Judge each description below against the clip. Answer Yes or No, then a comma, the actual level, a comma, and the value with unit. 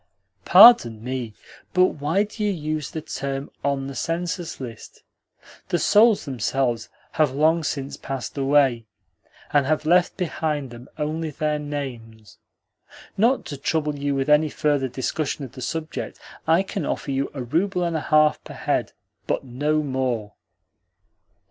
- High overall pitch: No, medium, 145 Hz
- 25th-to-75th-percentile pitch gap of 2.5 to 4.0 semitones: Yes, average, 3.3 semitones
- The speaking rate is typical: Yes, average, 150 wpm